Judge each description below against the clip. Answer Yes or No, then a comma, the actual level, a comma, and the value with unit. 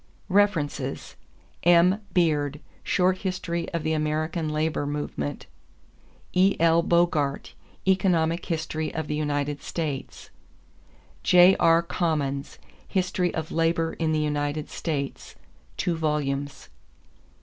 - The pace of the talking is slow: Yes, slow, 100 wpm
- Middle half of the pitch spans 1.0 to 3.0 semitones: Yes, average, 2.7 semitones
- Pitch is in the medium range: Yes, medium, 160 Hz